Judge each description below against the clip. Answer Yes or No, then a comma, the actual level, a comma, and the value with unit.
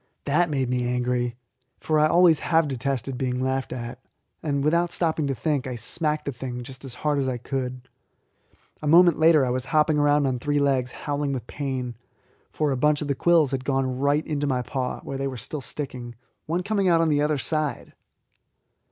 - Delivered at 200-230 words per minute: Yes, fast, 205 wpm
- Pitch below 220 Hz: Yes, medium, 140 Hz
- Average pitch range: Yes, average, 3.1 semitones